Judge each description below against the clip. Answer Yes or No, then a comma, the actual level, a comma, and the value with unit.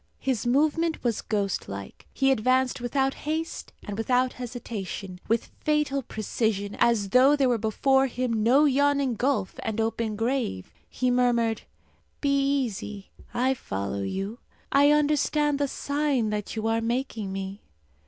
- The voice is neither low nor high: No, high, 245 Hz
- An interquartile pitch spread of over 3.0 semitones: Yes, average, 4.2 semitones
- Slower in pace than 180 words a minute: Yes, average, 145 wpm